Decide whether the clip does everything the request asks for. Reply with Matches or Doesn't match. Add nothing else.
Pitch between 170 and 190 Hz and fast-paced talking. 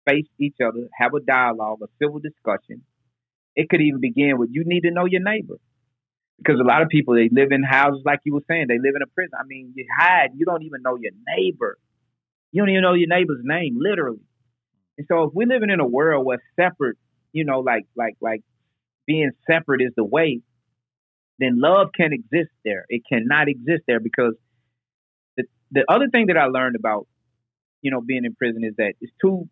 Doesn't match